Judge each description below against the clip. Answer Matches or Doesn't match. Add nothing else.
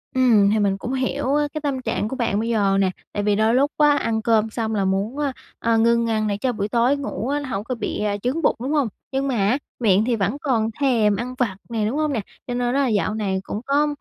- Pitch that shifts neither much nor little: Matches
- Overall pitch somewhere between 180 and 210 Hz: Doesn't match